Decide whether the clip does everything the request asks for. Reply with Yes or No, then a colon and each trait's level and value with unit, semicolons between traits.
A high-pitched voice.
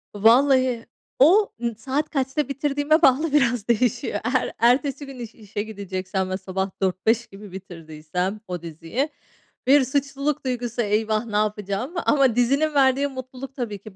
Yes: high, 240 Hz